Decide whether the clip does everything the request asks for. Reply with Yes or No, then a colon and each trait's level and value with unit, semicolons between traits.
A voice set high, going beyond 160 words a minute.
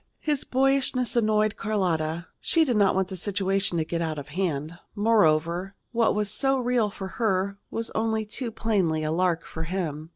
Yes: high, 195 Hz; average, 175 wpm